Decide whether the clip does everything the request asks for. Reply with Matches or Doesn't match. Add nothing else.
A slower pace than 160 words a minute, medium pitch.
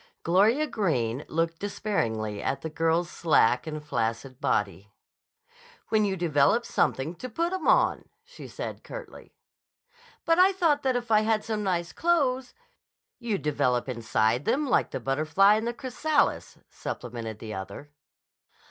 Matches